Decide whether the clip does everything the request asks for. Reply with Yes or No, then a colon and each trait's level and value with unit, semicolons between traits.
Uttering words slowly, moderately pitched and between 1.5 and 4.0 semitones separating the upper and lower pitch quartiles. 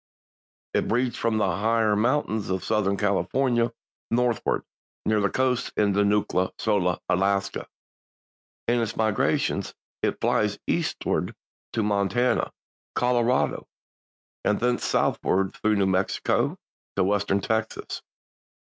No: slow, 110 wpm; low, 105 Hz; average, 3.0 semitones